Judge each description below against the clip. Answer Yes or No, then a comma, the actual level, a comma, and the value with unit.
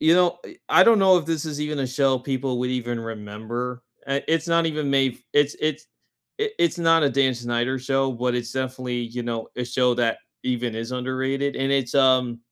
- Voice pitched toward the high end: No, low, 130 Hz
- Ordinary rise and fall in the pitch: Yes, average, 3.2 semitones